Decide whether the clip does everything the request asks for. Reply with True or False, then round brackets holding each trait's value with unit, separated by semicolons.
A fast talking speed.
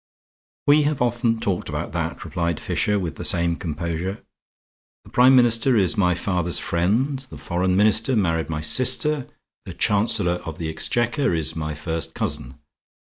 False (155 wpm)